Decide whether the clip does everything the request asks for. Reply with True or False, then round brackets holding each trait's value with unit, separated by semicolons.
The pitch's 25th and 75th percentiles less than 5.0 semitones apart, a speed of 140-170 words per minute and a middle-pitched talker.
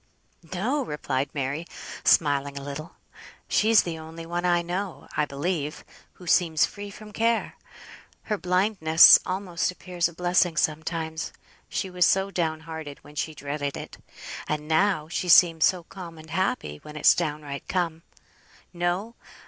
True (3.1 semitones; 145 wpm; 170 Hz)